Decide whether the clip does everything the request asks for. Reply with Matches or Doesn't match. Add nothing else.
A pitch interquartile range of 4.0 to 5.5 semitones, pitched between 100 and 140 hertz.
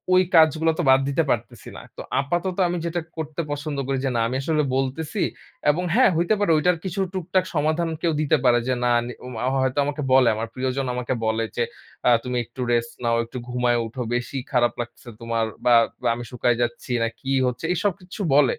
Matches